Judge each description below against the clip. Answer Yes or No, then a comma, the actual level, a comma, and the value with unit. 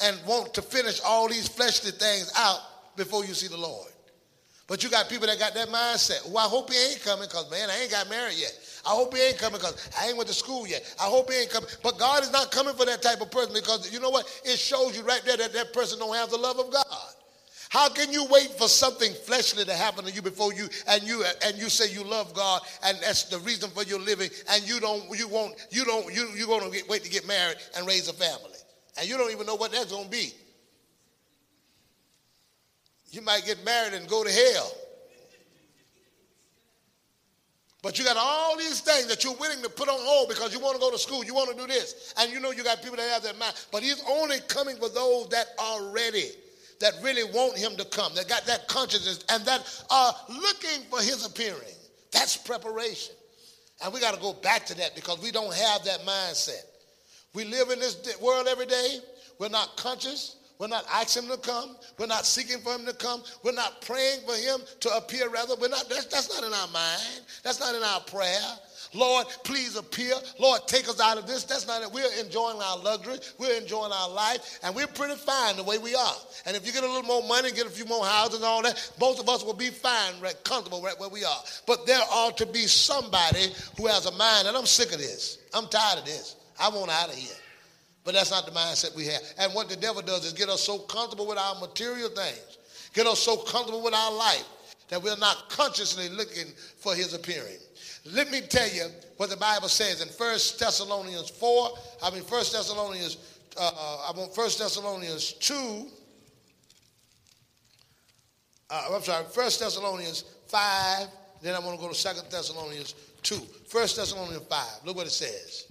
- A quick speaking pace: Yes, fast, 220 wpm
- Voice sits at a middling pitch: No, high, 230 Hz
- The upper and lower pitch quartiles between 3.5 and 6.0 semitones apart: Yes, average, 4.0 semitones